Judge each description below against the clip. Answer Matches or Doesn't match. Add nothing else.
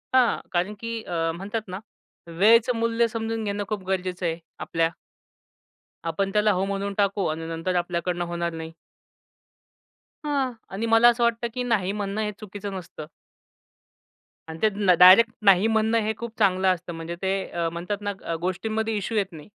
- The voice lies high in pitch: Matches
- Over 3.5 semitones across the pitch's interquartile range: Matches